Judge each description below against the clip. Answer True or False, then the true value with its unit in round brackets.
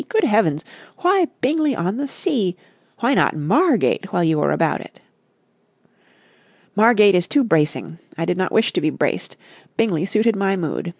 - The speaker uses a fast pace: False (165 wpm)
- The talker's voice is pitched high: True (205 Hz)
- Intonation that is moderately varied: False (6.8 semitones)